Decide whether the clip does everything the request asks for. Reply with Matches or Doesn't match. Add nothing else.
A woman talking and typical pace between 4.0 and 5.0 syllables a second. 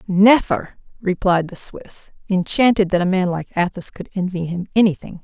Matches